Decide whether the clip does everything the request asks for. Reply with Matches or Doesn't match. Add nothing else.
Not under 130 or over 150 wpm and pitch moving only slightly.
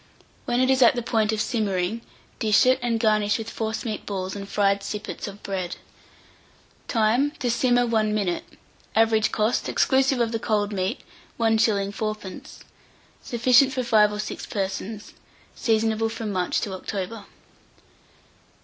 Matches